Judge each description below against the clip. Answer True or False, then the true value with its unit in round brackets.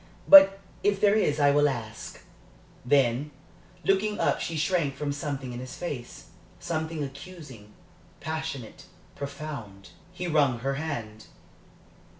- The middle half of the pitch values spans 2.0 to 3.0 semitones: False (4.2 semitones)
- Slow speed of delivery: True (125 wpm)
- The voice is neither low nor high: True (145 Hz)